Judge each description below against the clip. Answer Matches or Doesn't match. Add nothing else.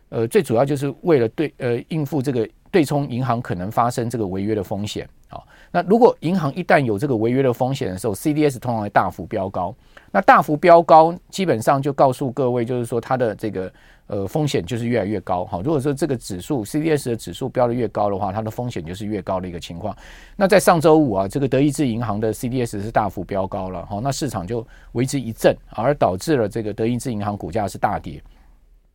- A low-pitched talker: Matches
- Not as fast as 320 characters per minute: Doesn't match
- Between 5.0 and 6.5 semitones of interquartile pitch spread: Matches